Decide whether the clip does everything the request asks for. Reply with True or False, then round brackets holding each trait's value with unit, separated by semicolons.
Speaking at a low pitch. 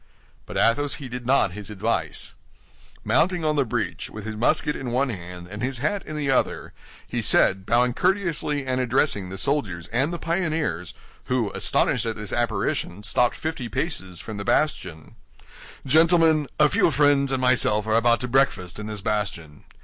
True (120 Hz)